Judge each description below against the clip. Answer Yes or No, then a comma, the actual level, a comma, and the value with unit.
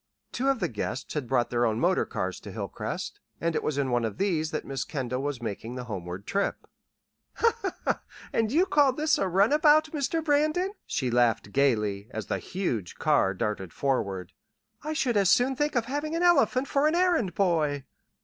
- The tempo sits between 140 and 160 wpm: No, average, 190 wpm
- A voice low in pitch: No, medium, 155 Hz